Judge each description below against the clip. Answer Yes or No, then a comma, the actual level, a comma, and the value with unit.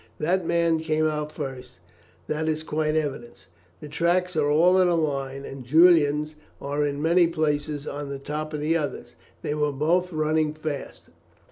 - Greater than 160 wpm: Yes, average, 170 wpm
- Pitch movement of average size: No, narrow, 1.9 semitones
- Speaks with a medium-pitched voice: Yes, medium, 155 Hz